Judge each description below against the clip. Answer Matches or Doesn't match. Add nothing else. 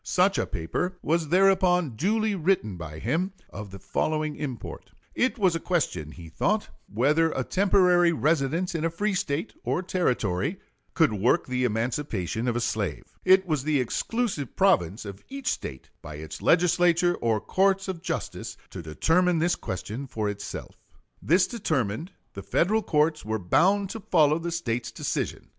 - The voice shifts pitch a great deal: Matches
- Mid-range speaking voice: Matches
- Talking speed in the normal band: Matches